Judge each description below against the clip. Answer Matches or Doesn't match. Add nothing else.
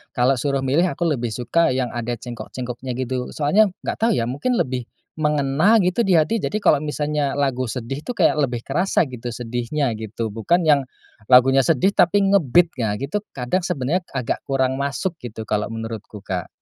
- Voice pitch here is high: Doesn't match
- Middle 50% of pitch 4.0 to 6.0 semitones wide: Matches